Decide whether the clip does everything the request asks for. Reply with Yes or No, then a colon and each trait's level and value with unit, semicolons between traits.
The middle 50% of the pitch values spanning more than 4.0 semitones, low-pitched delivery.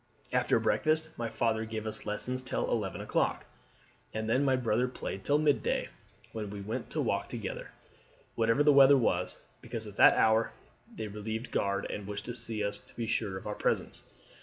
No: average, 3.2 semitones; low, 110 Hz